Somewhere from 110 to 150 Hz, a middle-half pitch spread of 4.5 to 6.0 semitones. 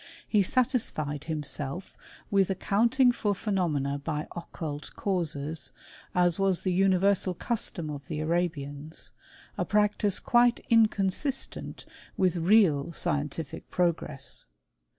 No: medium, 175 Hz; average, 5.0 semitones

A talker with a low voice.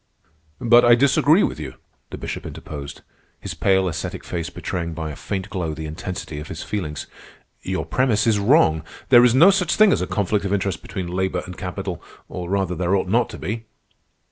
Yes: very low, 95 Hz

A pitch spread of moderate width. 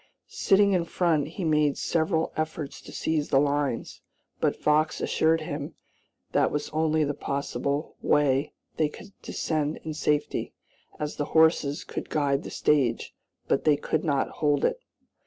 No: narrow, 1.7 semitones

